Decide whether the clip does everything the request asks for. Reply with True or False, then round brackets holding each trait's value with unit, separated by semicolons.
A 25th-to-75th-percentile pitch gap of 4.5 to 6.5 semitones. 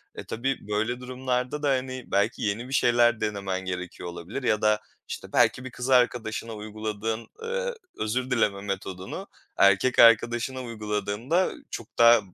False (3.4 semitones)